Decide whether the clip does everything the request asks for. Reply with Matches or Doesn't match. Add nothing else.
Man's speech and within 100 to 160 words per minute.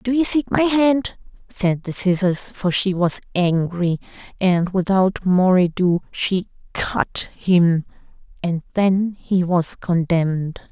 Doesn't match